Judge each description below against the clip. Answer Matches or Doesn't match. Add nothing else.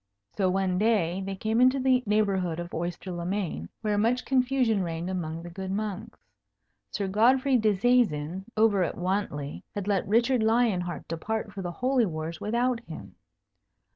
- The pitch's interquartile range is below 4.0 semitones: Doesn't match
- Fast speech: Doesn't match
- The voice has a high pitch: Matches